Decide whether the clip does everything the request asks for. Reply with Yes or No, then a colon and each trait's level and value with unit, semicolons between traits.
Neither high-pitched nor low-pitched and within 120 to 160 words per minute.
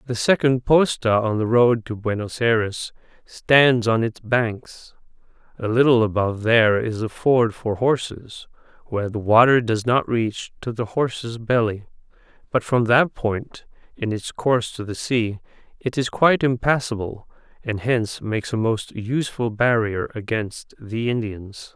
No: low, 115 Hz; average, 155 wpm